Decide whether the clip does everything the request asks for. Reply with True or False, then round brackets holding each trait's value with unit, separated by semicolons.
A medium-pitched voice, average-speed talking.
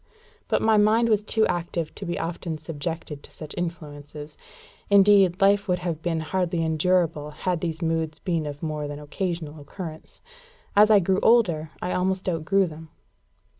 True (170 Hz; 165 wpm)